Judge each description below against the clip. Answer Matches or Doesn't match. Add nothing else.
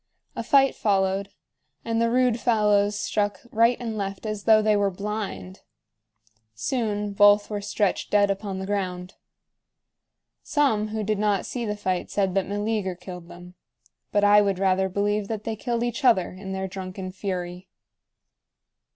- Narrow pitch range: Matches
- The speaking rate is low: Doesn't match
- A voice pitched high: Matches